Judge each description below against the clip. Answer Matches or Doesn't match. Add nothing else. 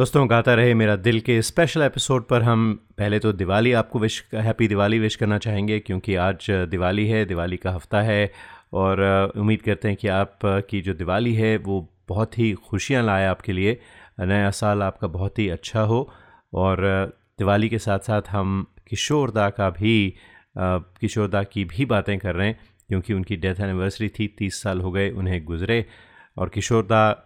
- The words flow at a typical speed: Matches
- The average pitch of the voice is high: Doesn't match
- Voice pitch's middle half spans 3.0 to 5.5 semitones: Doesn't match